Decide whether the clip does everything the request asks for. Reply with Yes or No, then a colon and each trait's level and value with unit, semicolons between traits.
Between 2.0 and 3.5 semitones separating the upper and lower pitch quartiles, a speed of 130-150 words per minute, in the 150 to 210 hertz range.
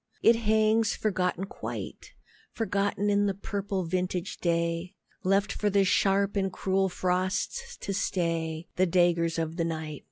Yes: average, 2.9 semitones; average, 140 wpm; high, 190 Hz